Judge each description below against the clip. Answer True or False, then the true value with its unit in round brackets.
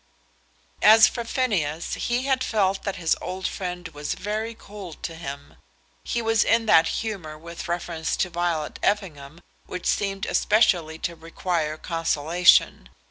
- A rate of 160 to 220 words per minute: False (140 wpm)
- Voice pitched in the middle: True (180 Hz)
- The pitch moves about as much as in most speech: True (4.5 semitones)